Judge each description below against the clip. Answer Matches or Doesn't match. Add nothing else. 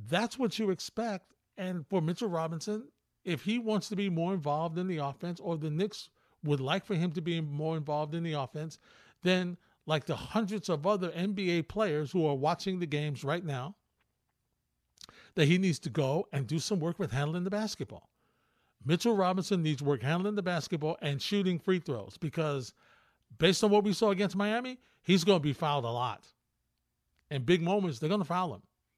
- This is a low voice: Doesn't match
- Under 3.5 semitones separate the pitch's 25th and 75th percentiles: Doesn't match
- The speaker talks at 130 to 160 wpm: Doesn't match